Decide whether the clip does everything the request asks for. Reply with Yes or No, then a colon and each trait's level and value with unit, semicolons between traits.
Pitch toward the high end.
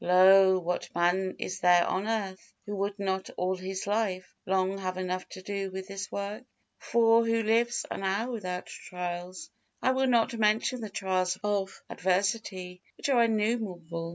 Yes: high, 195 Hz